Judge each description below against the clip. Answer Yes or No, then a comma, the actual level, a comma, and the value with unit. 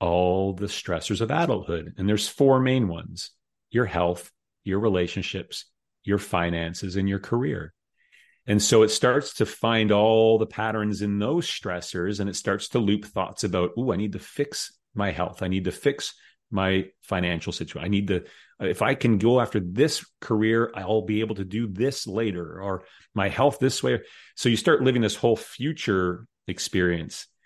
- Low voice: Yes, low, 105 Hz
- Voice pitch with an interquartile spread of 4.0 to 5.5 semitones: No, average, 3.5 semitones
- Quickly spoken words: No, average, 180 wpm